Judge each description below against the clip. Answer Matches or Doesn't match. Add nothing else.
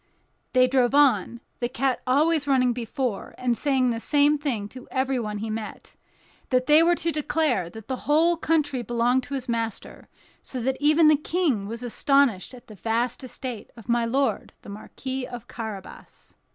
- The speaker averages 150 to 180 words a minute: Matches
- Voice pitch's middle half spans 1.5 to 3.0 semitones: Doesn't match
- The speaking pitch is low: Doesn't match